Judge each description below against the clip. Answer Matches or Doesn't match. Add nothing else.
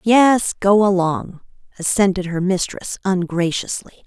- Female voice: Matches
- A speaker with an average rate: Doesn't match